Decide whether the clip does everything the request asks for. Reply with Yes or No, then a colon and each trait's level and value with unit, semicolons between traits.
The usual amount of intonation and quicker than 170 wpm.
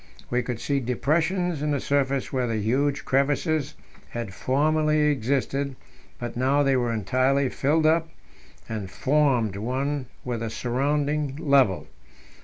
No: average, 3.1 semitones; slow, 135 wpm